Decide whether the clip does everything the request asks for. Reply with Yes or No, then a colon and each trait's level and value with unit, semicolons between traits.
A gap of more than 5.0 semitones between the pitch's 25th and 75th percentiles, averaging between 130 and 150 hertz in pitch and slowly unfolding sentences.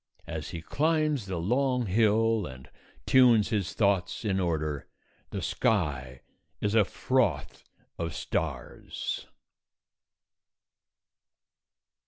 No: wide, 5.5 semitones; low, 100 Hz; slow, 95 wpm